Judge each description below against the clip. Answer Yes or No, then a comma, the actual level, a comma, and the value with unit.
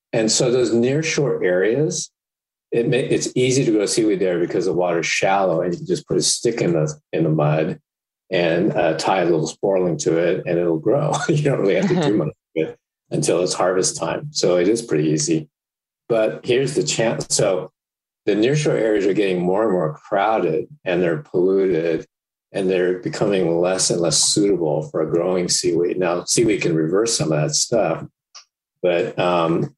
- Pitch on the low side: Yes, very low, 95 Hz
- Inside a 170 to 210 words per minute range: Yes, average, 200 wpm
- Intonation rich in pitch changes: Yes, wide, 8.6 semitones